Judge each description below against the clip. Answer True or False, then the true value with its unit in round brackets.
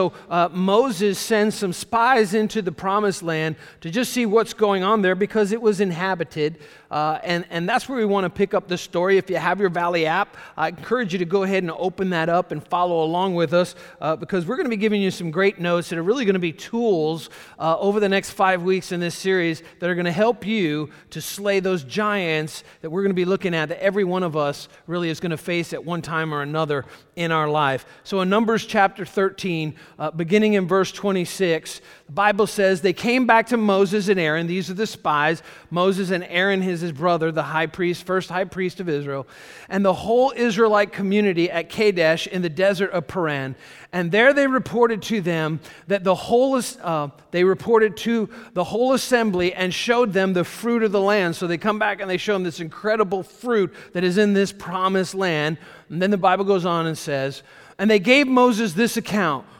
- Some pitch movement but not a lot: True (3.6 semitones)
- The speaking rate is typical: False (225 wpm)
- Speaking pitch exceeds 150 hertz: True (185 Hz)